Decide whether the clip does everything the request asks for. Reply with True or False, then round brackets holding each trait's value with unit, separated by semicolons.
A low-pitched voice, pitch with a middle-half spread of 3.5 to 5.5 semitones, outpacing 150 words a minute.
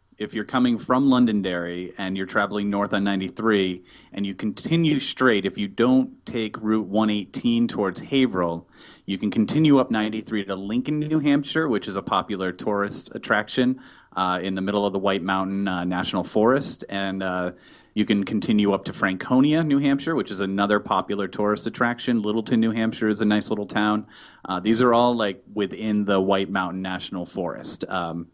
True (105 Hz; 3.8 semitones; 180 wpm)